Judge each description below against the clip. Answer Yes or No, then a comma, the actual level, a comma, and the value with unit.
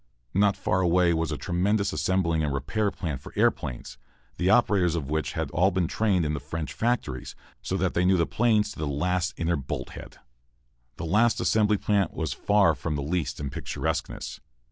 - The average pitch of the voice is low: Yes, very low, 90 Hz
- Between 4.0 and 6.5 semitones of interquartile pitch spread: Yes, average, 4.4 semitones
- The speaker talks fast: No, average, 185 wpm